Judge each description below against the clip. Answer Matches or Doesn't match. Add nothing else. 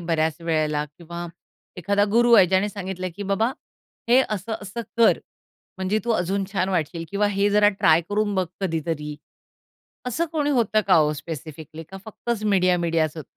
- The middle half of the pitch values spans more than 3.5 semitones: Matches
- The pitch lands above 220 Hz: Doesn't match